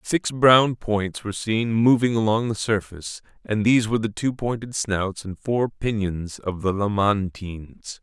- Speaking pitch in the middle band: No, low, 105 Hz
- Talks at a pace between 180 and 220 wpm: No, average, 165 wpm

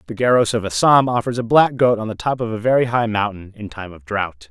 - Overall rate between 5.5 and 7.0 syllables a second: Yes, 5.9 syllables/s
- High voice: No, low, 110 Hz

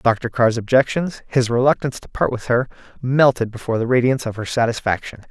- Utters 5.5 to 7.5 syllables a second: Yes, 6.0 syllables/s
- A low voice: Yes, low, 125 Hz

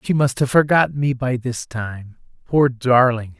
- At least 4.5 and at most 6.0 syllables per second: No, 4.3 syllables/s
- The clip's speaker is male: Yes, male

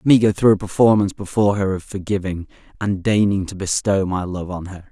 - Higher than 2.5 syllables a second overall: Yes, 5.8 syllables/s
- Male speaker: Yes, male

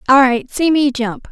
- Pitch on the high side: Yes, very high, 265 Hz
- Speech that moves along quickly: Yes, fast, 230 wpm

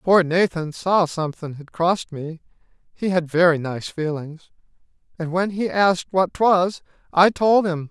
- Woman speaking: No, male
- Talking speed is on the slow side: No, average, 145 wpm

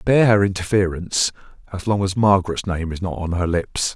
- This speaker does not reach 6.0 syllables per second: No, 6.2 syllables/s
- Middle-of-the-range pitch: No, very low, 95 Hz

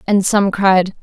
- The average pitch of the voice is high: Yes, high, 195 Hz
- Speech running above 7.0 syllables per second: No, 3.6 syllables/s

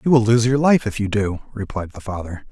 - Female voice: No, male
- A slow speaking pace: No, fast, 260 wpm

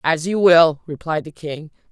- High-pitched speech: No, medium, 160 Hz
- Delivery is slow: No, average, 190 wpm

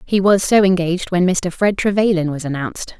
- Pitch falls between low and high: Yes, medium, 180 Hz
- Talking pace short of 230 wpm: Yes, average, 200 wpm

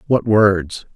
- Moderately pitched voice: No, low, 105 Hz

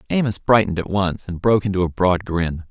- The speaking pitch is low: Yes, very low, 95 Hz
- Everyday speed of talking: No, fast, 220 wpm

